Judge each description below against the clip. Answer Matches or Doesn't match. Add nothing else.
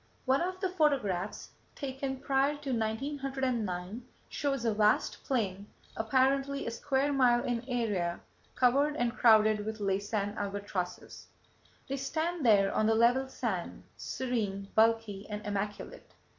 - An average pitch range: Matches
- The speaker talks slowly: Matches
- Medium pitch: Doesn't match